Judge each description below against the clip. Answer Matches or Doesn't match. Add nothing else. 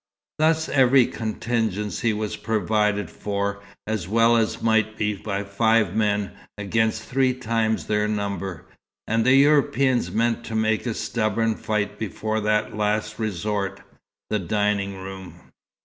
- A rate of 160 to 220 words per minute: Doesn't match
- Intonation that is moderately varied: Doesn't match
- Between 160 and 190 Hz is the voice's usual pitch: Doesn't match